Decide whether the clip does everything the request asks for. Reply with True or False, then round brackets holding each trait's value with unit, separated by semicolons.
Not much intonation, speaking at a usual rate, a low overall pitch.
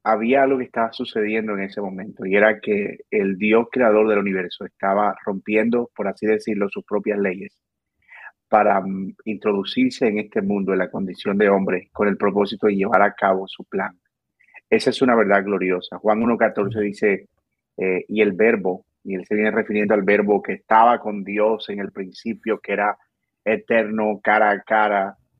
True (1.8 semitones; 175 wpm; 105 Hz)